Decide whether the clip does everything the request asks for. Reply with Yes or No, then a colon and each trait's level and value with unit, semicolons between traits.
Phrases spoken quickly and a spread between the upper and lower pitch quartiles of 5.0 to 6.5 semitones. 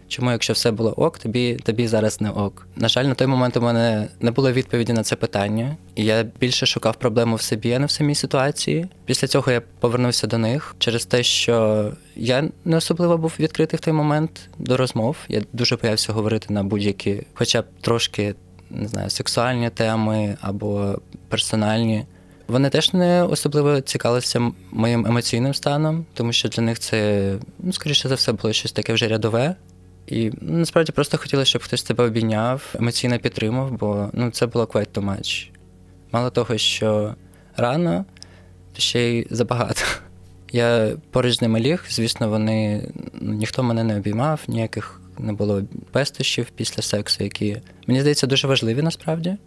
No: fast, 170 wpm; average, 3.6 semitones